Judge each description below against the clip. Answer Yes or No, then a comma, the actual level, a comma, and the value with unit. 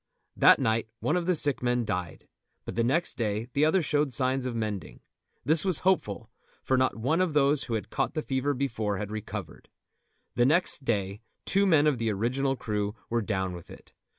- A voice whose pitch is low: Yes, low, 125 Hz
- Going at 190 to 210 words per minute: Yes, average, 200 wpm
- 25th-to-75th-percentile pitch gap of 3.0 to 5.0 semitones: No, wide, 5.4 semitones